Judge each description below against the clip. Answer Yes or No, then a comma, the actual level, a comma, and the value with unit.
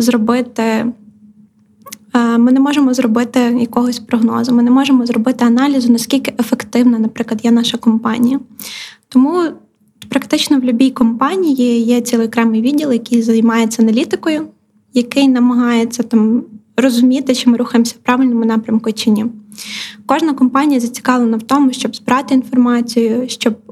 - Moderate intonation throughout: No, narrow, 2.0 semitones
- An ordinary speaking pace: Yes, average, 130 wpm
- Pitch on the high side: Yes, high, 240 Hz